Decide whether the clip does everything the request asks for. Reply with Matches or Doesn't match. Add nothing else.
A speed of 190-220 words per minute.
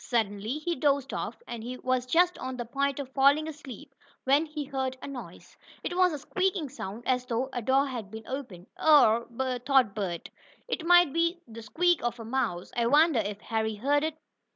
Matches